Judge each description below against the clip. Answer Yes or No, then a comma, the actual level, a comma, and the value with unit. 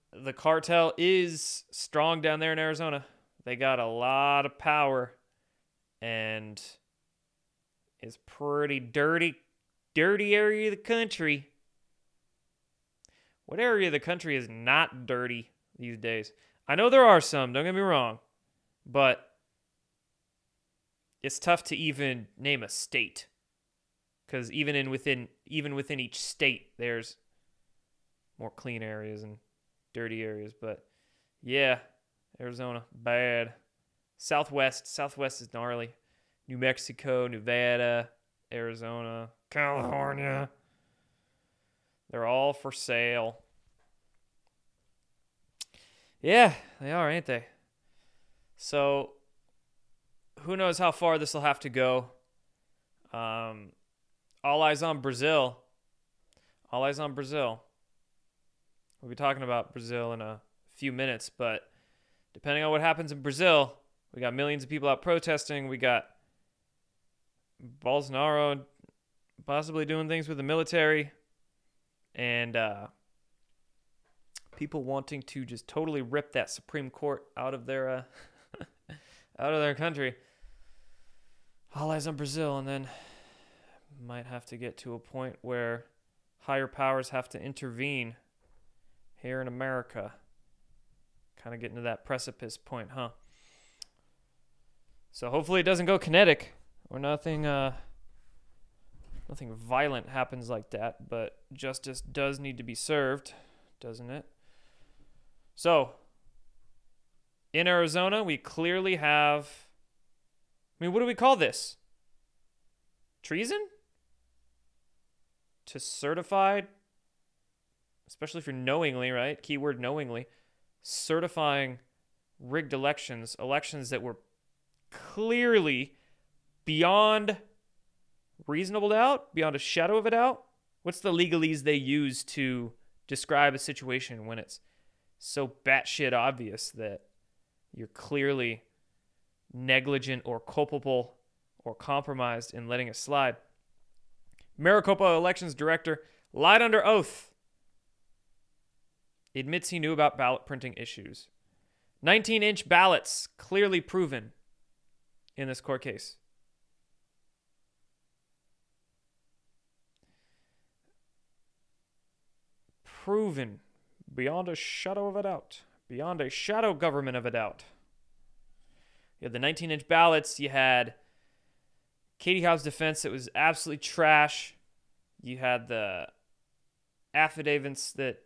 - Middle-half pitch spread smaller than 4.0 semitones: No, average, 4.4 semitones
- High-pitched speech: No, medium, 140 Hz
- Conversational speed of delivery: No, slow, 110 wpm